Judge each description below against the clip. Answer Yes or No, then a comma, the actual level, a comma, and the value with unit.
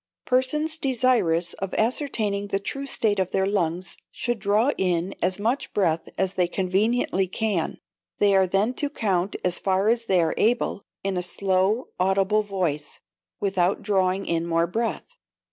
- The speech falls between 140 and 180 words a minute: Yes, average, 160 wpm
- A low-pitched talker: No, high, 195 Hz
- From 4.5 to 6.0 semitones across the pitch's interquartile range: No, average, 3.4 semitones